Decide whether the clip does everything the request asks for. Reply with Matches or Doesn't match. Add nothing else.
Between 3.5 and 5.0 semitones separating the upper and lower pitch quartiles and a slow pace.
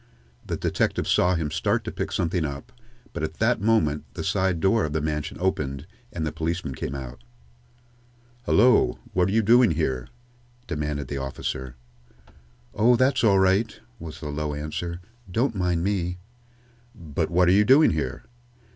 Doesn't match